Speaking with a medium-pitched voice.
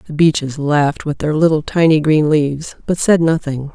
Yes: medium, 155 Hz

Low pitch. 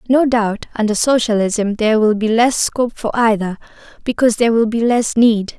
No: high, 225 Hz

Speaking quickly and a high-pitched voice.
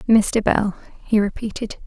No: slow, 130 wpm; high, 210 Hz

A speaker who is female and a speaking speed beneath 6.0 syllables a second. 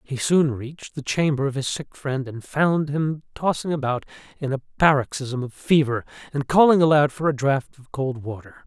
No: male; 5.1 syllables/s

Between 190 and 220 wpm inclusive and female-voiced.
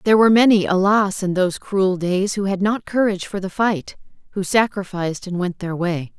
Yes: fast, 205 wpm; female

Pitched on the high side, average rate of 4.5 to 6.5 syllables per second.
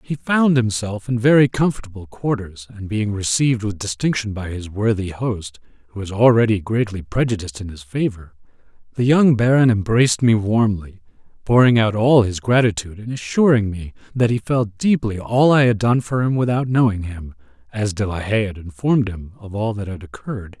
No: low, 110 Hz; 5.3 syllables/s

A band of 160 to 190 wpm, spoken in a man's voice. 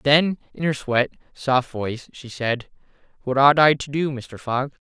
Yes: average, 185 wpm; male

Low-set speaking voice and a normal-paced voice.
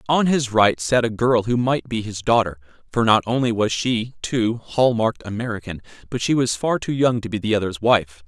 No: low, 110 Hz; fast, 225 wpm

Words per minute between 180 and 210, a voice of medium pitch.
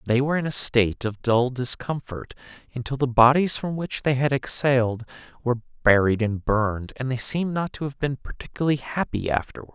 No: average, 185 wpm; low, 130 Hz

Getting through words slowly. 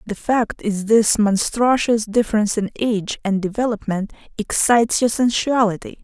Yes: slow, 130 wpm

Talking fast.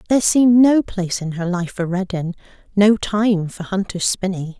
No: average, 185 wpm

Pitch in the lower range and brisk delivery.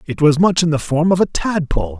No: medium, 160 Hz; fast, 270 wpm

